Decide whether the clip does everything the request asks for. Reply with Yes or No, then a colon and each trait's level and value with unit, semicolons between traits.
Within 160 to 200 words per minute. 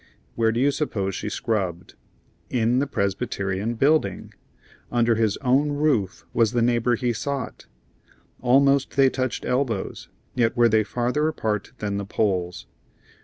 No: average, 140 wpm